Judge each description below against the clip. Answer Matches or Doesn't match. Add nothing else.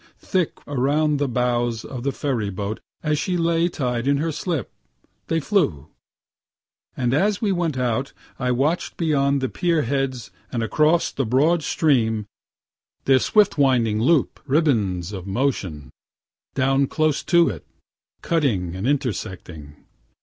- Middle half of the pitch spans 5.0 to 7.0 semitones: Matches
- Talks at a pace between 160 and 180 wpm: Doesn't match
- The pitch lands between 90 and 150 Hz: Matches